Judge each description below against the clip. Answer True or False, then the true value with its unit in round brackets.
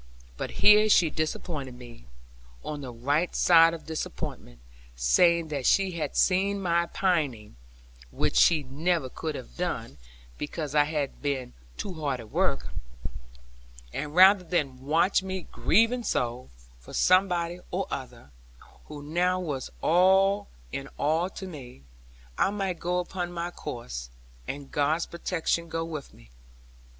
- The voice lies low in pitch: False (160 Hz)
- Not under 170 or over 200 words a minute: False (140 wpm)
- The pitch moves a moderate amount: True (4.7 semitones)